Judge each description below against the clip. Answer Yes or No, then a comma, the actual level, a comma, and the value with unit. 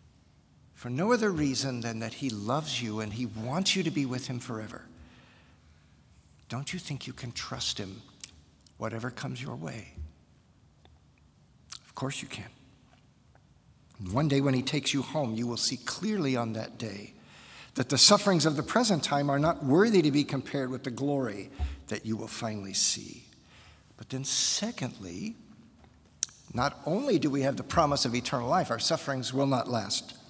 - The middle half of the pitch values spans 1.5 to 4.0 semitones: No, average, 4.4 semitones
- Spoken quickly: No, average, 170 wpm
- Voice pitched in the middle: No, low, 130 Hz